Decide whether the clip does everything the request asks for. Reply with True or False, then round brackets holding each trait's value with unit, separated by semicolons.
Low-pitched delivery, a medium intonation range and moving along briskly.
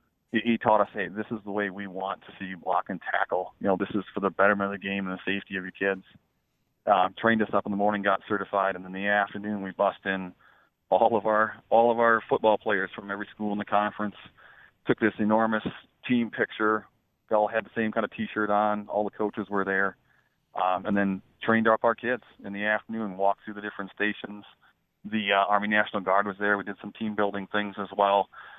False (105 Hz; 1.6 semitones; 235 wpm)